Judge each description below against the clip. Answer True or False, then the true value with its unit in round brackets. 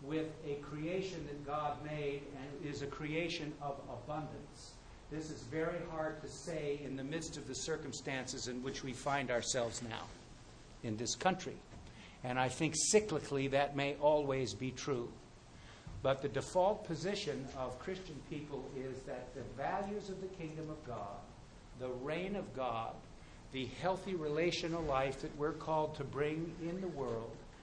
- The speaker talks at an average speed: True (160 wpm)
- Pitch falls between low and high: True (145 Hz)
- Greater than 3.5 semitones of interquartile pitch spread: False (3.2 semitones)